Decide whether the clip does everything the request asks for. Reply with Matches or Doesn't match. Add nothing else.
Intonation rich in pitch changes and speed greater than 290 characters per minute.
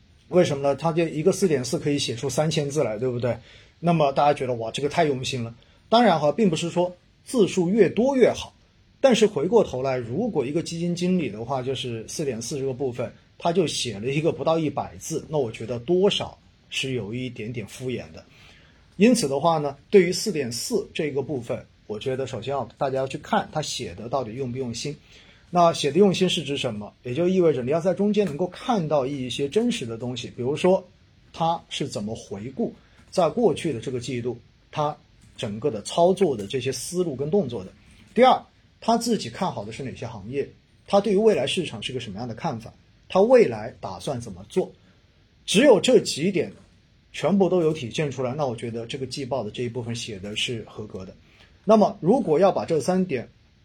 Matches